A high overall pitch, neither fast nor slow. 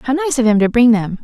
No: high, 240 Hz; fast, 340 wpm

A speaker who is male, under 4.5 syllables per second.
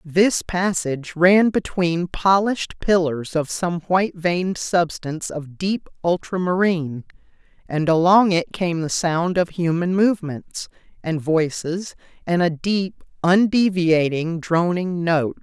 No: female; 4.0 syllables/s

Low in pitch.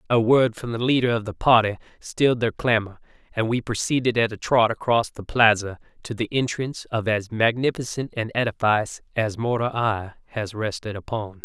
Yes: low, 115 Hz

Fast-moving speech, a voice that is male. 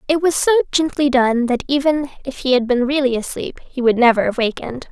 No: fast, 220 wpm; female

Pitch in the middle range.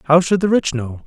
Yes: medium, 160 Hz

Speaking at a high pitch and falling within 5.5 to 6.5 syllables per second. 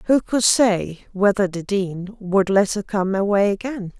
No: high, 200 Hz; 4.1 syllables/s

